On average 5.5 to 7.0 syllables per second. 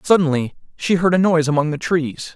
Yes: 5.9 syllables/s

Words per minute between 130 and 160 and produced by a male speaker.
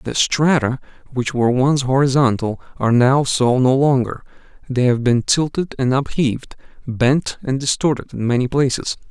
Yes: average, 145 wpm; male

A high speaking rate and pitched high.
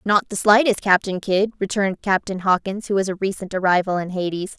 No: average, 195 wpm; high, 195 Hz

